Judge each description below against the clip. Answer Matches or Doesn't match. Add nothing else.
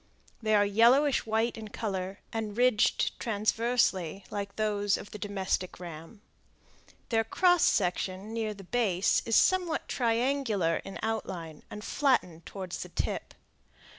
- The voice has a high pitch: Matches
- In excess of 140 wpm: Doesn't match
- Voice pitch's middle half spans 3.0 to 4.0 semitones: Matches